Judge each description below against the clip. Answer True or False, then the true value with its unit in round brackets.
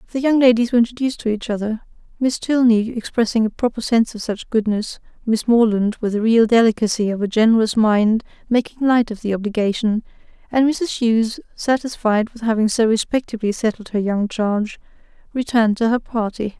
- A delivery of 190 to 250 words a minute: False (175 wpm)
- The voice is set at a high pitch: True (225 Hz)